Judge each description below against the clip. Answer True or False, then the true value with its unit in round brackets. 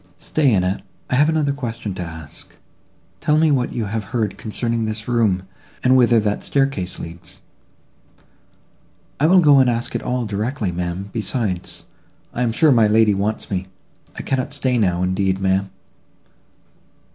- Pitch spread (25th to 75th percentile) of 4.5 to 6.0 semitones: True (4.9 semitones)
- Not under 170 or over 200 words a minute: False (160 wpm)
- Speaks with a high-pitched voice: False (110 Hz)